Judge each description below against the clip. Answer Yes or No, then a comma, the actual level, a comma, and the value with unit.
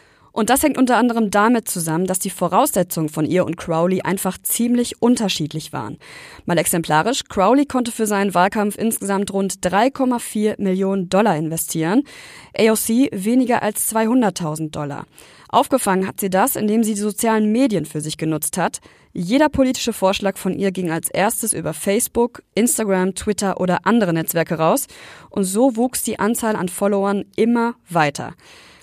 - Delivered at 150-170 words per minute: Yes, average, 155 wpm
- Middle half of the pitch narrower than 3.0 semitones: No, average, 4.4 semitones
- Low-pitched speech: No, high, 200 Hz